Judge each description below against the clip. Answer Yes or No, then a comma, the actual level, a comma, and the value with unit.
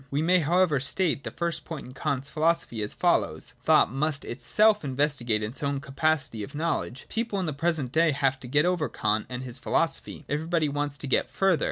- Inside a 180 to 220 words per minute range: Yes, average, 200 wpm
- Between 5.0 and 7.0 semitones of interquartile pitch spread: No, average, 4.0 semitones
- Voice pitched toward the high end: No, medium, 145 Hz